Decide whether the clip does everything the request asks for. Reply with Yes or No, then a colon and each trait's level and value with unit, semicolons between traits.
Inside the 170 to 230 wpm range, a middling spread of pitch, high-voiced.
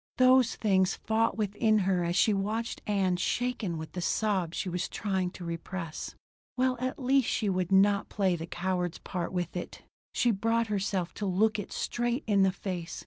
Yes: average, 185 wpm; average, 3.6 semitones; high, 195 Hz